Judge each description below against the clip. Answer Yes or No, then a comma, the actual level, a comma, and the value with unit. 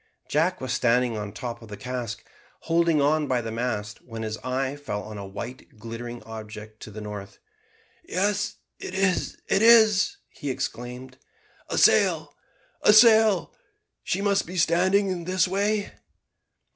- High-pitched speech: No, low, 130 Hz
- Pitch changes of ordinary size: No, wide, 8.8 semitones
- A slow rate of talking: No, average, 155 wpm